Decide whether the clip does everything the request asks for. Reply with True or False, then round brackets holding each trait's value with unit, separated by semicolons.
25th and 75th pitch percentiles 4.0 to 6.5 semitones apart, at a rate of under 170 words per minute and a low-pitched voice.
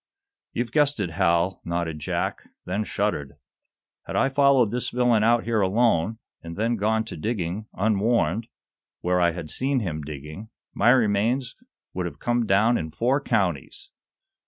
True (5.6 semitones; 155 wpm; 105 Hz)